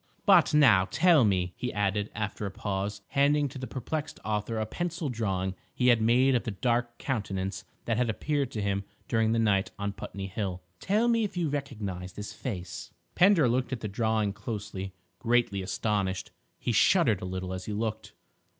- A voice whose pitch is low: Yes, low, 110 Hz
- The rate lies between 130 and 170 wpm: No, average, 180 wpm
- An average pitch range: Yes, average, 4.8 semitones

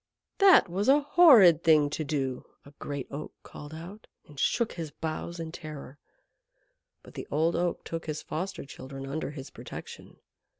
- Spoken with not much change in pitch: No, average, 3.5 semitones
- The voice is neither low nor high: Yes, medium, 160 Hz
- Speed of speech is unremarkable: Yes, average, 165 wpm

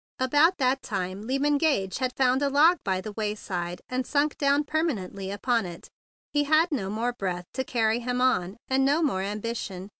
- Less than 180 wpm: No, average, 185 wpm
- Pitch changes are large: Yes, wide, 6.2 semitones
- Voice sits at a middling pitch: No, very high, 250 Hz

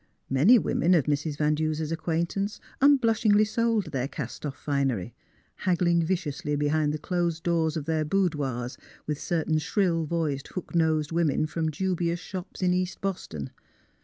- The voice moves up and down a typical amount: Yes, average, 3.3 semitones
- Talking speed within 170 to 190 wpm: No, average, 155 wpm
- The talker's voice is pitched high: No, medium, 160 Hz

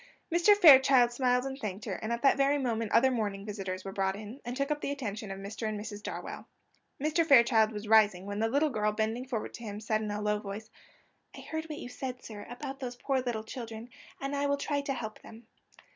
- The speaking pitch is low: No, high, 230 Hz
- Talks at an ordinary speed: No, fast, 235 wpm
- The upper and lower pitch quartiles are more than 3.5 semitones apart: Yes, average, 4.2 semitones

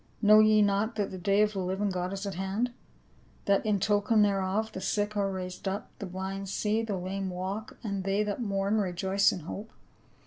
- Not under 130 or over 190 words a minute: No, fast, 205 wpm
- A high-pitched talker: Yes, high, 200 Hz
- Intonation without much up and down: Yes, narrow, 1.7 semitones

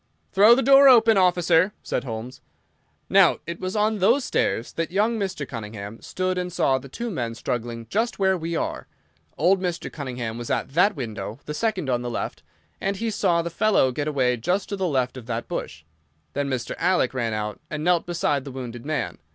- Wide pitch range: Yes, wide, 7.7 semitones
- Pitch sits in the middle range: Yes, medium, 155 Hz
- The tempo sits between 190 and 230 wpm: Yes, average, 195 wpm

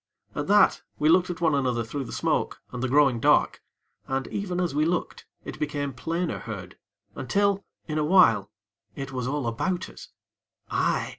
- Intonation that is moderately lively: No, wide, 5.9 semitones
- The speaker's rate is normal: Yes, average, 175 wpm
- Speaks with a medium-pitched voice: Yes, medium, 145 Hz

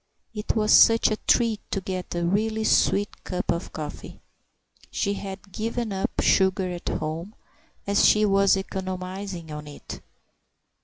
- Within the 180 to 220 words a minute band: No, average, 145 wpm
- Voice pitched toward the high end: Yes, high, 195 Hz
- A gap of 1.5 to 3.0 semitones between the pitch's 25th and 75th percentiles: Yes, average, 2.7 semitones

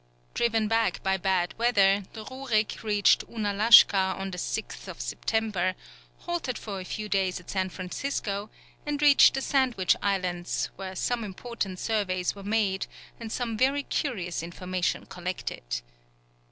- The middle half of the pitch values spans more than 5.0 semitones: No, average, 3.6 semitones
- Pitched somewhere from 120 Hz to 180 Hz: No, high, 200 Hz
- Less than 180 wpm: Yes, average, 140 wpm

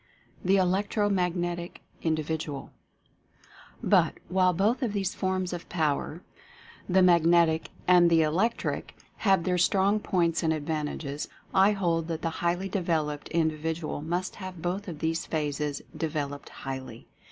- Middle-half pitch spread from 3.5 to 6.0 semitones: No, average, 3.0 semitones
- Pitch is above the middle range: No, medium, 170 Hz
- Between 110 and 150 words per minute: Yes, average, 140 wpm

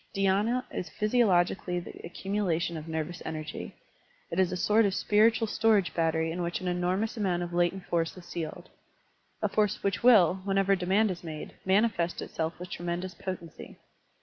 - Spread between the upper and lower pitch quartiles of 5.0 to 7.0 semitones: No, average, 2.7 semitones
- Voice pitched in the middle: Yes, medium, 180 Hz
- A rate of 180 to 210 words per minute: No, average, 170 wpm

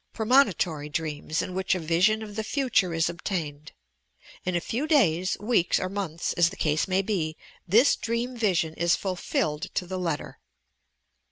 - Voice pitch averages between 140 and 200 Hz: Yes, medium, 185 Hz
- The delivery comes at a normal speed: Yes, average, 165 wpm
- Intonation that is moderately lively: Yes, average, 4.8 semitones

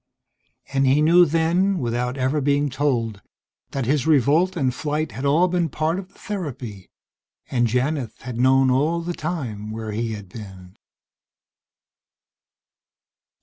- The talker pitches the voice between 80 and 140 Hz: Yes, low, 135 Hz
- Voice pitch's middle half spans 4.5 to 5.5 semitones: Yes, average, 5.2 semitones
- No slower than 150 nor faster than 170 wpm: No, average, 140 wpm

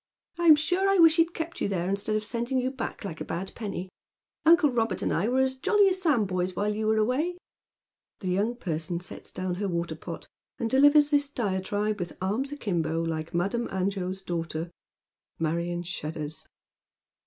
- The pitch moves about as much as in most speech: No, wide, 7.0 semitones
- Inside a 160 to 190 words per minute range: Yes, average, 175 wpm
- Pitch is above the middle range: Yes, high, 205 Hz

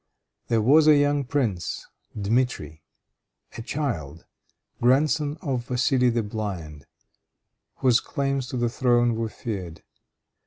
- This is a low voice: Yes, low, 120 Hz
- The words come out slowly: Yes, slow, 115 wpm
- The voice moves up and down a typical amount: Yes, average, 4.6 semitones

